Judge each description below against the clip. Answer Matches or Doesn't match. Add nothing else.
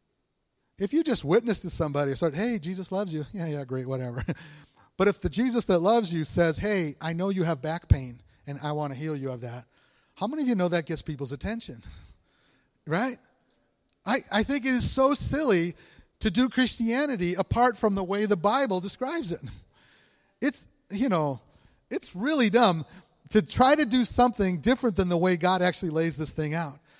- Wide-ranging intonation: Matches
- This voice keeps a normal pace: Matches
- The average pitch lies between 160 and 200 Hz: Matches